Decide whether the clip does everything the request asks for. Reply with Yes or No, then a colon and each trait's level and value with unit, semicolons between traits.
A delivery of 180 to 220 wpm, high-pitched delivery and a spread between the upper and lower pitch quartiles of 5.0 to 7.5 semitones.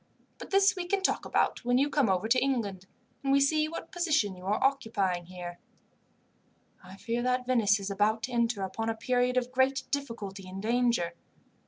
Yes: average, 190 wpm; high, 235 Hz; average, 5.3 semitones